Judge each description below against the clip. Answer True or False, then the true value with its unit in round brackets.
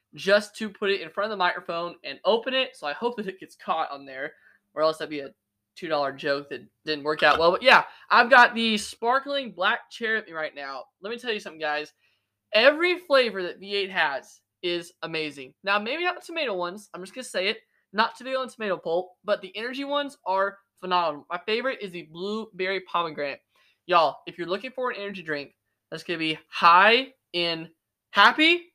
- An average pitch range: False (6.5 semitones)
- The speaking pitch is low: False (185 Hz)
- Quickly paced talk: True (215 wpm)